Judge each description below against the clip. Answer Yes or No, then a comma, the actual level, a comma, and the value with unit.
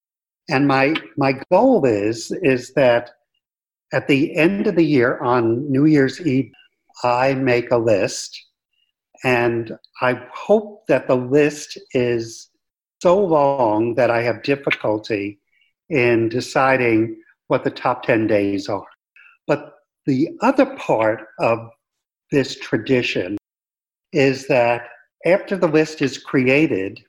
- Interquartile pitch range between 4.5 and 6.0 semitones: No, average, 4.1 semitones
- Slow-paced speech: Yes, slow, 125 wpm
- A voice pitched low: Yes, low, 130 Hz